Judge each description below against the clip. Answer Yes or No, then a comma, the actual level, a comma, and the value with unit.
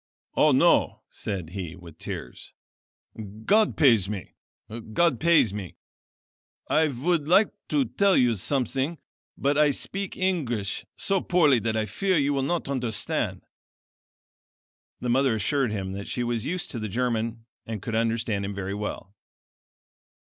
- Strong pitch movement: Yes, wide, 6.4 semitones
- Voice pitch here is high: No, low, 120 Hz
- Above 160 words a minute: No, average, 145 wpm